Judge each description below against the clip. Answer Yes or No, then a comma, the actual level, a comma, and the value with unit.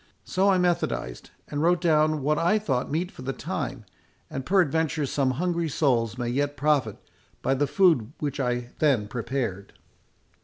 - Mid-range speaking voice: Yes, medium, 145 Hz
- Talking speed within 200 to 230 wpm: No, average, 160 wpm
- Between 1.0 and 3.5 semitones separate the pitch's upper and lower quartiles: No, average, 4.8 semitones